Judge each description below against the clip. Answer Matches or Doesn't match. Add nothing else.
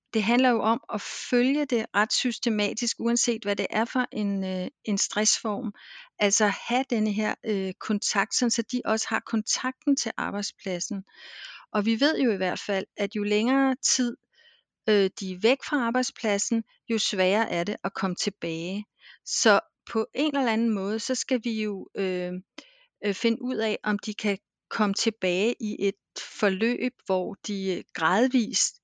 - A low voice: Doesn't match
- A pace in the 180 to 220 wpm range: Doesn't match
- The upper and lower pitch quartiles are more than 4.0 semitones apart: Doesn't match